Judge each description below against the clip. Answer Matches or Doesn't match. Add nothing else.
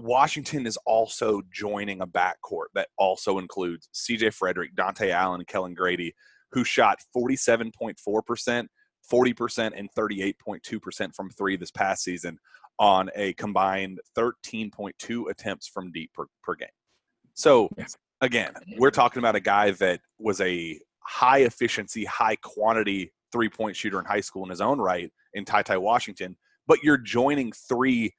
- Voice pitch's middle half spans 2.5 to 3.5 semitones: Doesn't match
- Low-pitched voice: Matches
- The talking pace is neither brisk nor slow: Matches